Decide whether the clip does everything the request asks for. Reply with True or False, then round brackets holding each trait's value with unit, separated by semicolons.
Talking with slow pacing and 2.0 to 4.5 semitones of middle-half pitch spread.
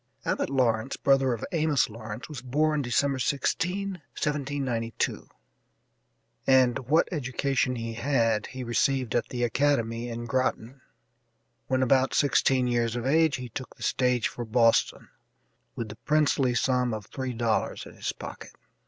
False (145 wpm; 2.9 semitones)